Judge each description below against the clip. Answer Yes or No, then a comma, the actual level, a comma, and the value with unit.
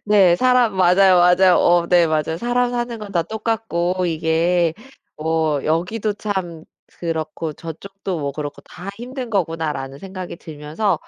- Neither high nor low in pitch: Yes, medium, 175 Hz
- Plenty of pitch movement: No, average, 4.1 semitones